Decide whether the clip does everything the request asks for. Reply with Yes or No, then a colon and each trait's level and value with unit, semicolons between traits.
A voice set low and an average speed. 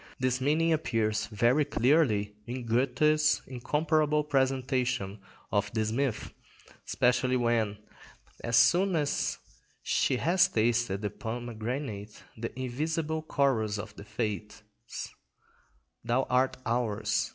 No: low, 125 Hz; slow, 105 wpm